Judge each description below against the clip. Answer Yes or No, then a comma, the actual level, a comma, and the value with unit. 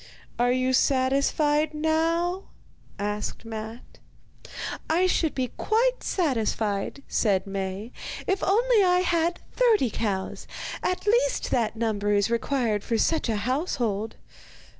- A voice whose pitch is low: No, very high, 260 Hz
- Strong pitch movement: Yes, wide, 8.0 semitones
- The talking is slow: Yes, slow, 120 wpm